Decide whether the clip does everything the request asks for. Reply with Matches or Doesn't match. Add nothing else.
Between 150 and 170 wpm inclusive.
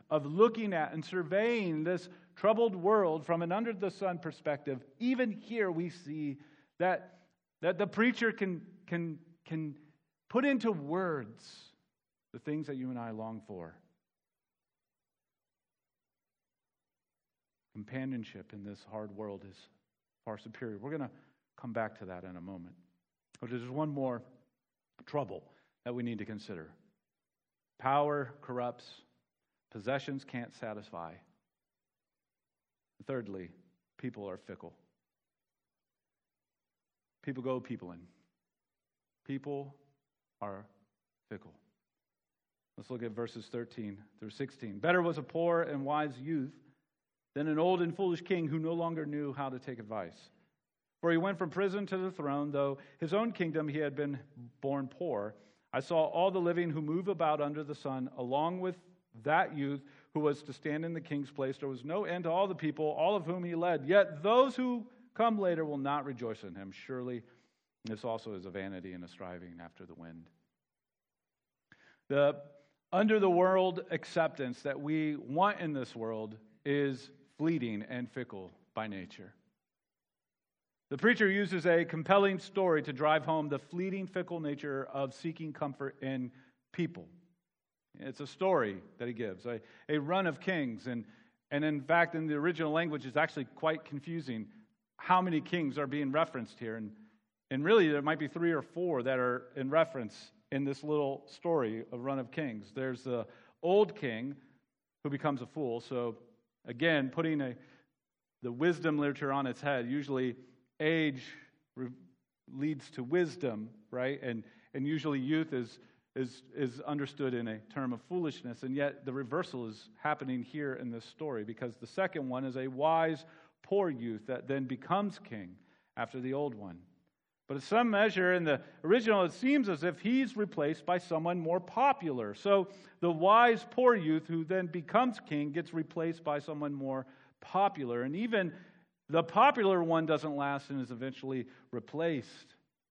Matches